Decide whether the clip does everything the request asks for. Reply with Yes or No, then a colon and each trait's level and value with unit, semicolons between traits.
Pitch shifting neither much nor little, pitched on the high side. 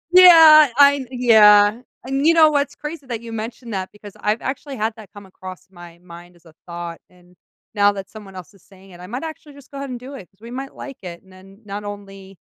No: wide, 6.1 semitones; high, 210 Hz